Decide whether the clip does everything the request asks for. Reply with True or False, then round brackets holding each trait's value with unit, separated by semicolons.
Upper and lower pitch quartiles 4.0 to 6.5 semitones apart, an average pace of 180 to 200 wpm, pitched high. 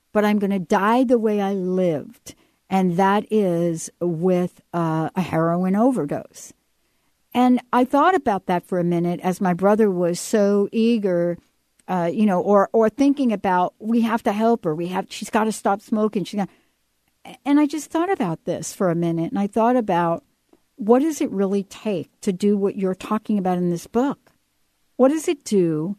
True (4.3 semitones; 190 wpm; 200 Hz)